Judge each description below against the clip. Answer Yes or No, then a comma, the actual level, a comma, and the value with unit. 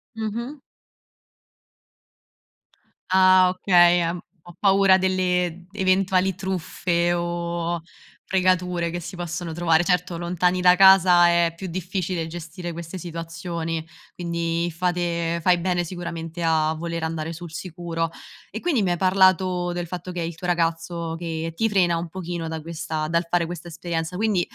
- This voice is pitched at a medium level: Yes, medium, 175 Hz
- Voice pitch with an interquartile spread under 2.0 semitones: Yes, narrow, 1.6 semitones